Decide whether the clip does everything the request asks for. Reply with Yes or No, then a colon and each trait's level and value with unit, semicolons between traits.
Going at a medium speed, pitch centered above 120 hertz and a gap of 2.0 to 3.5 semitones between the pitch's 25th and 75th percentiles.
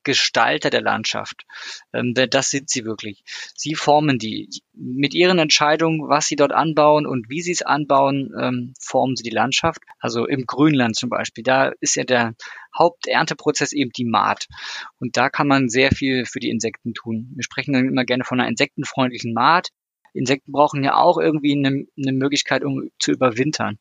Yes: average, 175 wpm; low, 135 Hz; average, 3.1 semitones